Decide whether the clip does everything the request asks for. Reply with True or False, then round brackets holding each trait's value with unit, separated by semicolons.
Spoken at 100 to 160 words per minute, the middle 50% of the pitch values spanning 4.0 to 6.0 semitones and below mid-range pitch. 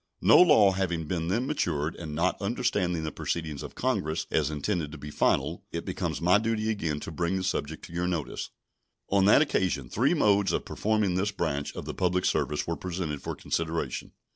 False (195 wpm; 4.3 semitones; 90 Hz)